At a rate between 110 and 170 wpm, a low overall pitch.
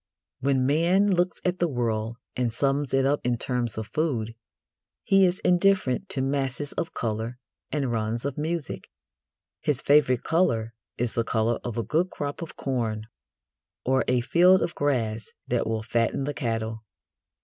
Yes: average, 160 wpm; low, 130 Hz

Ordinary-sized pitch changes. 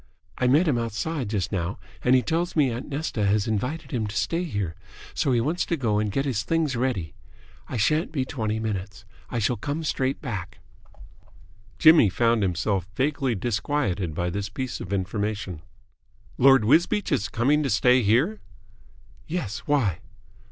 No: wide, 5.9 semitones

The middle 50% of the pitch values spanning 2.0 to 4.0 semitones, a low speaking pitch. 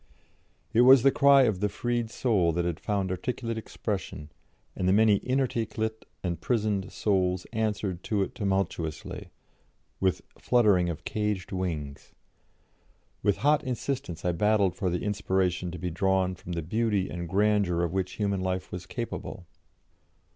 Yes: average, 3.5 semitones; low, 100 Hz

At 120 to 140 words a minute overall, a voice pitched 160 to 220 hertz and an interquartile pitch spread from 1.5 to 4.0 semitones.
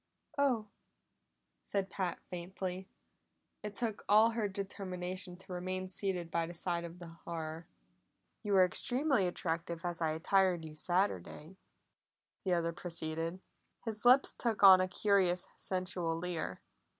Yes: slow, 135 wpm; medium, 185 Hz; average, 2.7 semitones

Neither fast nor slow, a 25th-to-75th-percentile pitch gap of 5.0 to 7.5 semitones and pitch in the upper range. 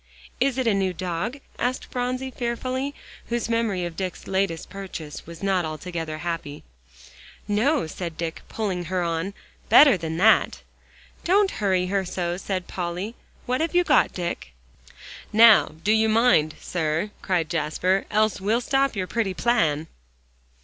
Yes: average, 150 wpm; average, 5.3 semitones; high, 195 Hz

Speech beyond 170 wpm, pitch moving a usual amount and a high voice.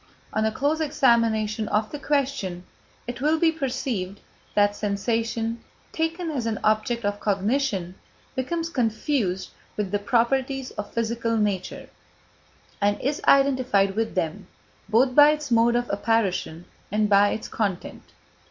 No: slow, 135 wpm; average, 4.6 semitones; high, 230 Hz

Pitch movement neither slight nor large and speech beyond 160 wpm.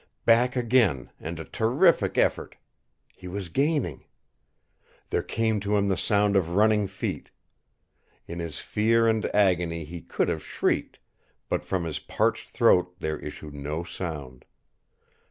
No: average, 5.0 semitones; average, 140 wpm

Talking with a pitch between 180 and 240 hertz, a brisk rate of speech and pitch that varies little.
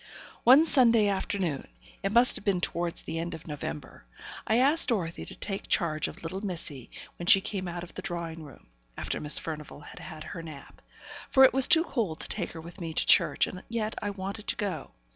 No: medium, 185 Hz; fast, 215 wpm; average, 4.6 semitones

